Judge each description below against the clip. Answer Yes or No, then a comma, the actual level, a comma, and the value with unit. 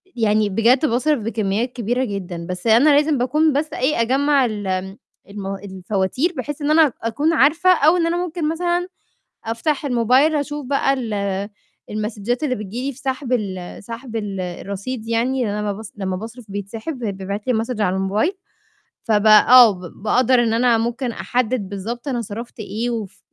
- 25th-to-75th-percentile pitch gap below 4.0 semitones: No, average, 4.8 semitones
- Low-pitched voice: No, high, 235 Hz